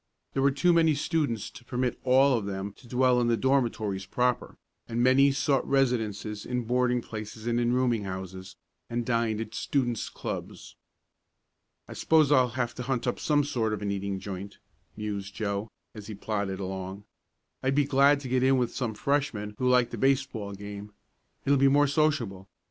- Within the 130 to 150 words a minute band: No, average, 180 wpm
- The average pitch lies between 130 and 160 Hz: No, low, 120 Hz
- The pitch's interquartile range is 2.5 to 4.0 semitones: No, average, 4.4 semitones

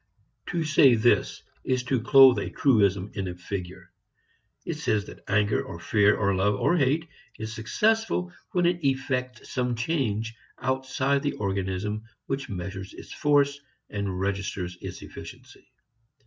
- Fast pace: No, average, 145 wpm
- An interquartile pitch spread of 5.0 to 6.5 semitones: Yes, wide, 5.5 semitones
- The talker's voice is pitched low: Yes, low, 115 Hz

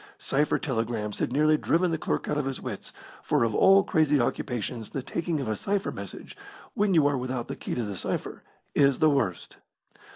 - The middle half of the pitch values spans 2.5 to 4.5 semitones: No, average, 5.0 semitones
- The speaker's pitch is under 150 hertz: Yes, low, 135 Hz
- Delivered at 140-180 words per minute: No, average, 200 wpm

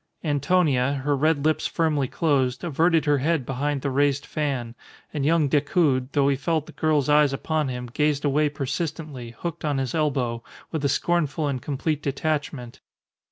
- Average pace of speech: Yes, average, 165 wpm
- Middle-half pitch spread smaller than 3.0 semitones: Yes, narrow, 2.5 semitones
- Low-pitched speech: No, medium, 145 Hz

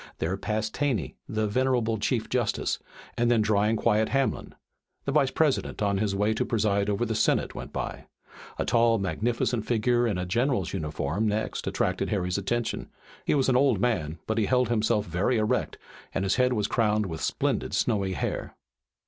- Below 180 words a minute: No, average, 185 wpm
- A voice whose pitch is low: Yes, low, 110 Hz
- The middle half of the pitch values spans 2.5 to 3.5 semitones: Yes, average, 3.2 semitones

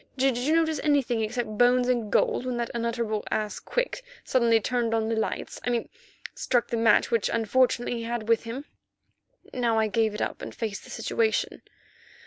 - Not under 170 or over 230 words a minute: Yes, average, 180 wpm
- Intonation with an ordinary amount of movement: No, narrow, 2.0 semitones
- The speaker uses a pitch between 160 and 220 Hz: No, high, 235 Hz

